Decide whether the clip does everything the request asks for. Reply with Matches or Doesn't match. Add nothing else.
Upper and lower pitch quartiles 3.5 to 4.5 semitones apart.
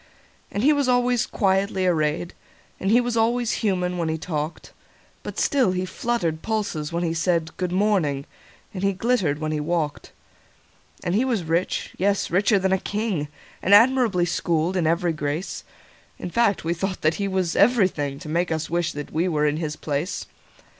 Matches